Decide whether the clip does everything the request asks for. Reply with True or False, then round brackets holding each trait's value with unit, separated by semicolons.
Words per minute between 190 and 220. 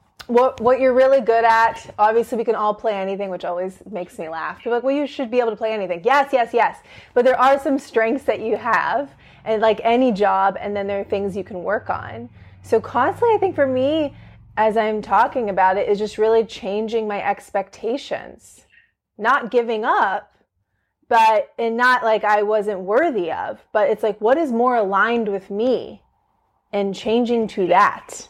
True (195 wpm)